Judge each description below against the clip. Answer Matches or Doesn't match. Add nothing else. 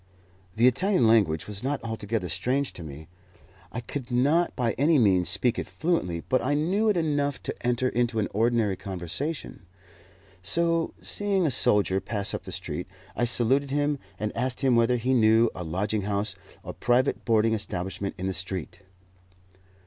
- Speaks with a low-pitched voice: Matches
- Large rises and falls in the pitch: Matches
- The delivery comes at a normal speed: Matches